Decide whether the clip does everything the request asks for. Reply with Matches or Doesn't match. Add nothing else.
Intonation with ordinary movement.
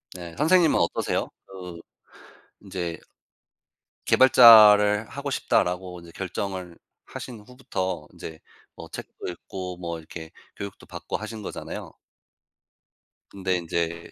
Matches